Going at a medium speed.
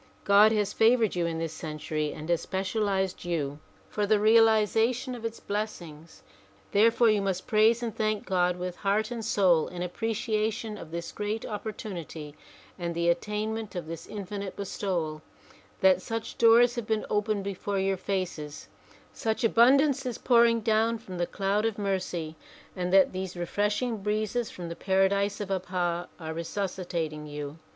Yes: average, 160 wpm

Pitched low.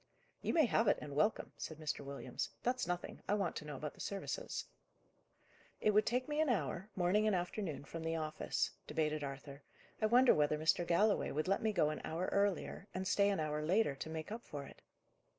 No: medium, 175 Hz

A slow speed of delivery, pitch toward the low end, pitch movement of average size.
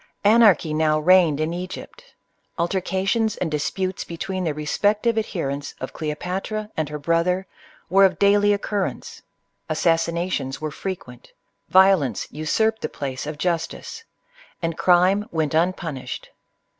No: slow, 125 wpm; medium, 175 Hz; average, 4.0 semitones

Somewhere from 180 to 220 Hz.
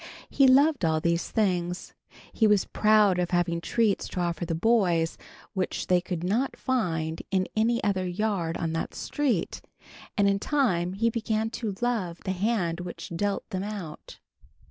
Yes: high, 190 Hz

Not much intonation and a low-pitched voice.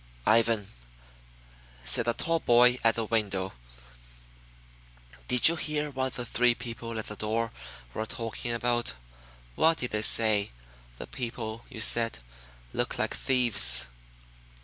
Yes: narrow, 2.1 semitones; low, 115 Hz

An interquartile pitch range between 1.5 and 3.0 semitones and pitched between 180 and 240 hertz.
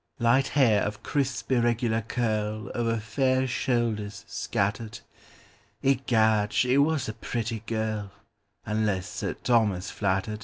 No: narrow, 2.6 semitones; low, 110 Hz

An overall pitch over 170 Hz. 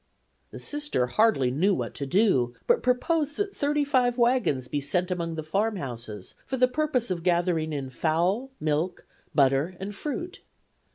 Yes: medium, 185 Hz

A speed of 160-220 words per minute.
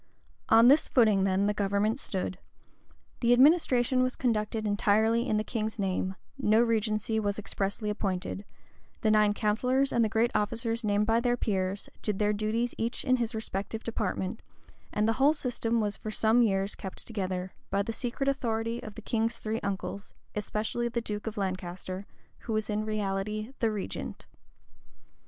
Yes: average, 165 wpm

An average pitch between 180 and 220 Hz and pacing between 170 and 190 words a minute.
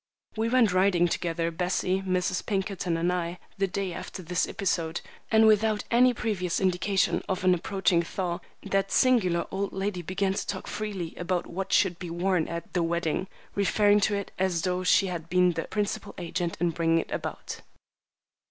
Yes: medium, 185 Hz; average, 175 wpm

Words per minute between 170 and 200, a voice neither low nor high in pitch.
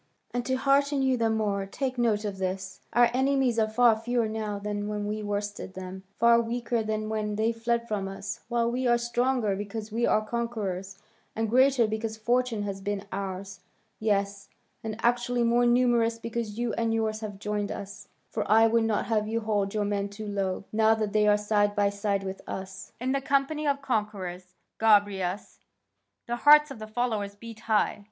No: average, 190 wpm; high, 220 Hz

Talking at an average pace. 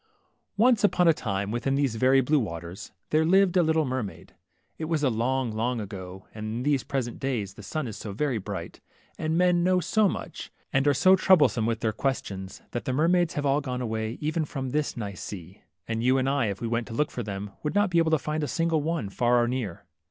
No: fast, 240 wpm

